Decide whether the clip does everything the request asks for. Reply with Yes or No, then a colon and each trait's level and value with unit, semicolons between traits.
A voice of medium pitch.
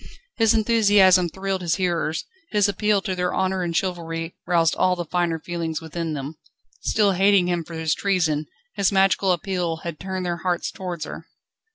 Yes: medium, 180 Hz